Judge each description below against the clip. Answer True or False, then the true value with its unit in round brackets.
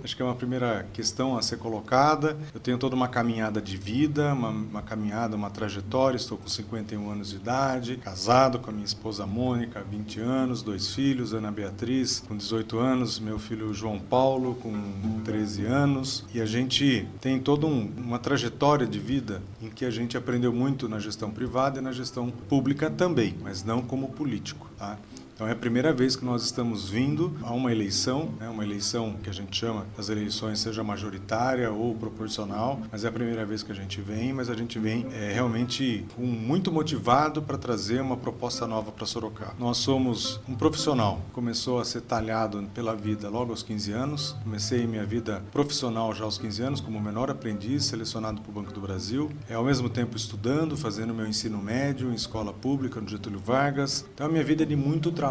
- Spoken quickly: True (195 wpm)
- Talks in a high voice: False (115 Hz)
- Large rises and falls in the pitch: False (3.2 semitones)